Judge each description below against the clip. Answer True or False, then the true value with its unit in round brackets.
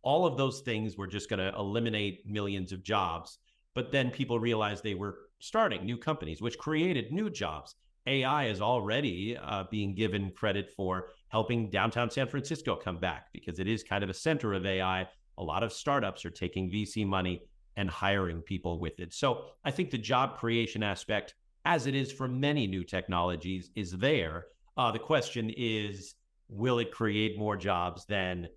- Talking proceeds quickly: False (185 wpm)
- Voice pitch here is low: True (105 Hz)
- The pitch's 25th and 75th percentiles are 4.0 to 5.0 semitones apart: True (4.4 semitones)